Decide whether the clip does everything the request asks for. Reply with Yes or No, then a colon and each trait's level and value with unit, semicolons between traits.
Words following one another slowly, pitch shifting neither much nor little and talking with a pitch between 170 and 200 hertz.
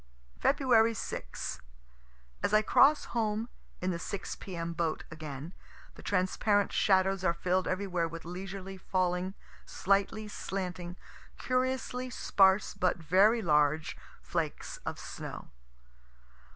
Yes: slow, 115 wpm; average, 3.3 semitones; high, 190 Hz